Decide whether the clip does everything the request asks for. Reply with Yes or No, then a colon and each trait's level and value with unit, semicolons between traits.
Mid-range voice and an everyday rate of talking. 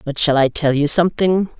No: medium, 155 Hz; fast, 225 wpm